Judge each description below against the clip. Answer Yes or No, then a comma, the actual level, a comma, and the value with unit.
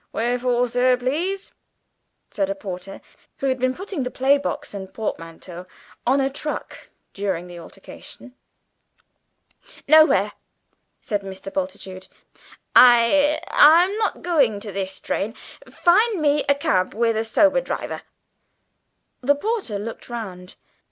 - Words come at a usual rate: No, slow, 125 wpm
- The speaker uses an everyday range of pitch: No, wide, 6.8 semitones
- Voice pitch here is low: No, very high, 250 Hz